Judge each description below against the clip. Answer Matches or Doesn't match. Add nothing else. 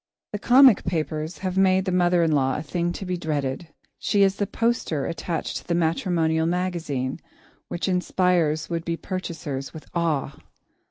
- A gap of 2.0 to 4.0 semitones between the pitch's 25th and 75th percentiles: Matches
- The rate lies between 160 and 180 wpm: Matches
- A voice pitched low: Doesn't match